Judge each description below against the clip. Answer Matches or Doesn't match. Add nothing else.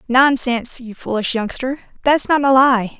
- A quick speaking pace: Doesn't match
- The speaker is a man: Doesn't match